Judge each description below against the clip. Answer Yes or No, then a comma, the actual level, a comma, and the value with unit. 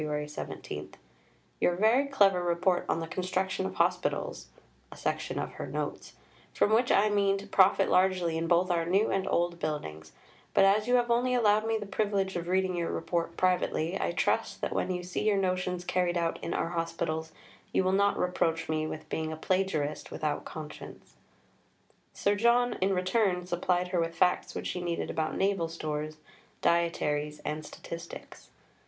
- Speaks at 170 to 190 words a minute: Yes, average, 175 wpm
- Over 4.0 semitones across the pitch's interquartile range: No, average, 2.9 semitones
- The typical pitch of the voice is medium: Yes, medium, 180 Hz